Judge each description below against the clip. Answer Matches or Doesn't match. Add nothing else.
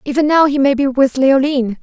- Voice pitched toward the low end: Doesn't match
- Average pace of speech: Doesn't match